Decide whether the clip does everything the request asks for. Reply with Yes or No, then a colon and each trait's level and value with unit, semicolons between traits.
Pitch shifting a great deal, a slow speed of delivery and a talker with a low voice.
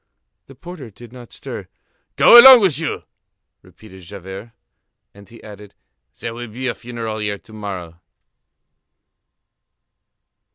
No: average, 3.7 semitones; slow, 125 wpm; low, 110 Hz